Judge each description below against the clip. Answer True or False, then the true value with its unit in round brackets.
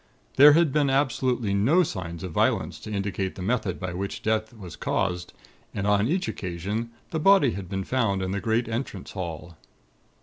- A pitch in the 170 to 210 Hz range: False (105 Hz)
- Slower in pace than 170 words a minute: False (180 wpm)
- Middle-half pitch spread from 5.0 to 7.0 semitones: True (5.3 semitones)